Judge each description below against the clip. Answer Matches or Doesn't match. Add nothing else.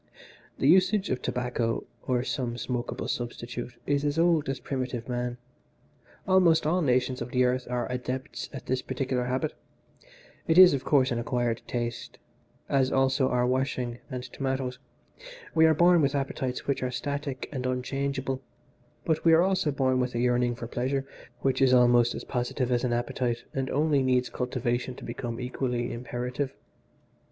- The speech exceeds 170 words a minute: Doesn't match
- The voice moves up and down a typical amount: Doesn't match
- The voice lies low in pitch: Matches